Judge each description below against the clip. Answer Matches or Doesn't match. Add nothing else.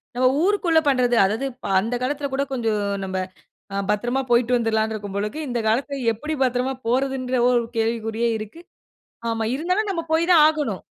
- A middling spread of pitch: Matches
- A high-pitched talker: Matches